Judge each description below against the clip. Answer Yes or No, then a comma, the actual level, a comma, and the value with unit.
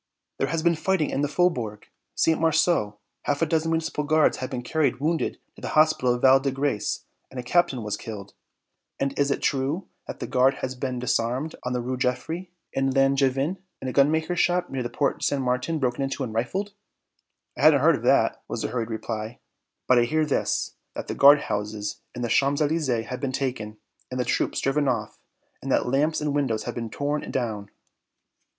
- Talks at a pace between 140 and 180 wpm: No, fast, 205 wpm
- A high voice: No, low, 135 Hz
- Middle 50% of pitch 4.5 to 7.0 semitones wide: No, average, 3.9 semitones